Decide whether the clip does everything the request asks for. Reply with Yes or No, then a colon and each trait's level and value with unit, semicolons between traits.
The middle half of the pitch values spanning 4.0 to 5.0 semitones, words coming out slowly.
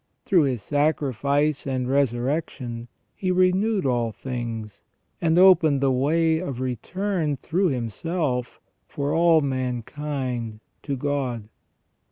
Yes: average, 4.6 semitones; slow, 110 wpm